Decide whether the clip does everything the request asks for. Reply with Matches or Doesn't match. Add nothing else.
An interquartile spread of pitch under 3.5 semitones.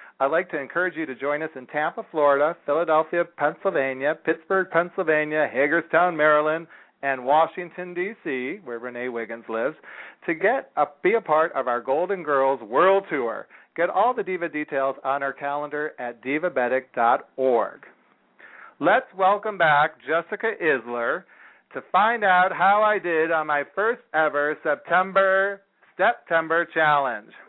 Doesn't match